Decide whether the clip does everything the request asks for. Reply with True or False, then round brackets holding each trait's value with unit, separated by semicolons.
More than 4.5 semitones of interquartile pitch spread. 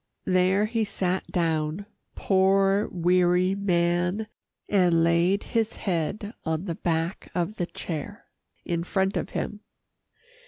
False (2.6 semitones)